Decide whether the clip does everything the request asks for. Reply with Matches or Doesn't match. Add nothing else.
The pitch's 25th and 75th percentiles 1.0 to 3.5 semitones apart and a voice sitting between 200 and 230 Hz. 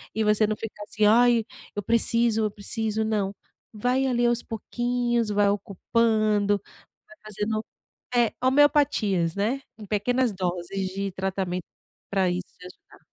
Matches